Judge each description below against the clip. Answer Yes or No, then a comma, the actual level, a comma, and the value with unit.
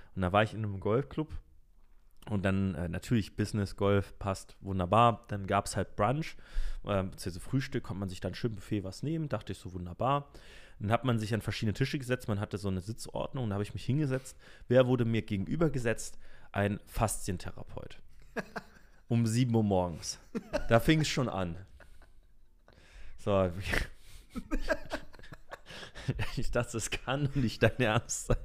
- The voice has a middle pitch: No, low, 105 Hz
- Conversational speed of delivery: Yes, average, 165 wpm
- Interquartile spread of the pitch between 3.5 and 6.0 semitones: Yes, average, 4.1 semitones